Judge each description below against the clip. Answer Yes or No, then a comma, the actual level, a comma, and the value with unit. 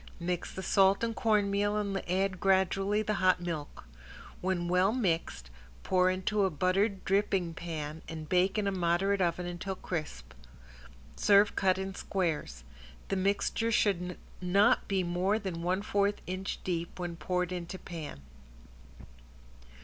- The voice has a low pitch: No, medium, 185 Hz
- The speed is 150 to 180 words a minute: No, average, 140 wpm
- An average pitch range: No, narrow, 2.3 semitones